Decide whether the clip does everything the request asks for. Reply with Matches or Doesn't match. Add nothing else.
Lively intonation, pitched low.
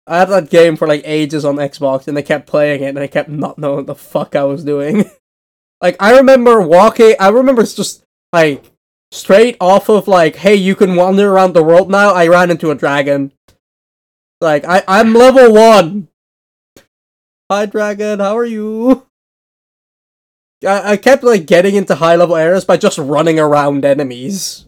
Doesn't match